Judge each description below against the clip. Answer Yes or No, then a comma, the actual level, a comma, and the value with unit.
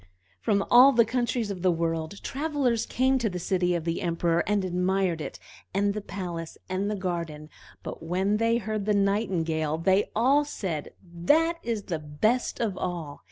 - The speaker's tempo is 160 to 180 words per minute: Yes, average, 175 wpm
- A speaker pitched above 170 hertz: Yes, high, 190 Hz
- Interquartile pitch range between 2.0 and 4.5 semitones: No, average, 5.0 semitones